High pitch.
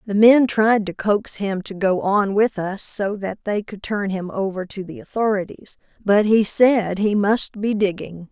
Yes: high, 200 Hz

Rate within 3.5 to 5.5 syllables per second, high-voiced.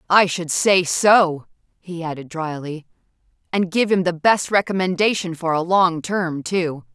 No: 4.2 syllables/s; medium, 175 Hz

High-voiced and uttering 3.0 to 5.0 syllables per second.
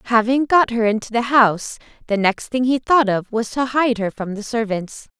Yes: high, 230 Hz; 4.9 syllables/s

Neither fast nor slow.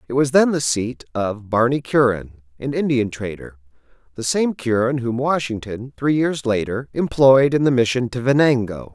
Yes: average, 160 wpm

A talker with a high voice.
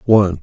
No: low, 100 Hz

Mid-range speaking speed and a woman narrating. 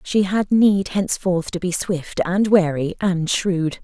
Yes: average, 170 wpm; female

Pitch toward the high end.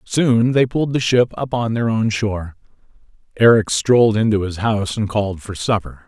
No: low, 110 Hz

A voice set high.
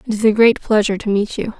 Yes: high, 215 Hz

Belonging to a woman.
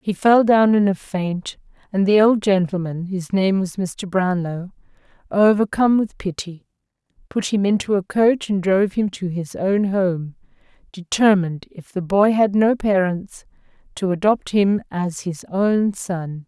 Yes: female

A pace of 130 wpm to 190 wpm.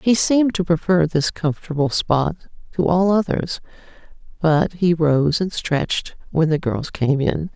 Yes: average, 160 wpm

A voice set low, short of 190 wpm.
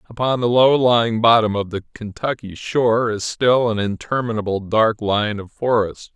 Yes: low, 110 Hz; average, 165 wpm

